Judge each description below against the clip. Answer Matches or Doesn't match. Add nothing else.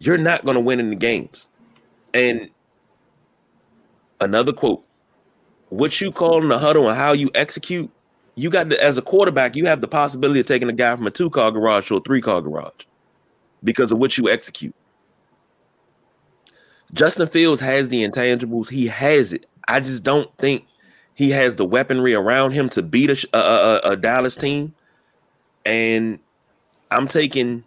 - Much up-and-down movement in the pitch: Doesn't match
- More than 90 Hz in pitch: Matches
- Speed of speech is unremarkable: Matches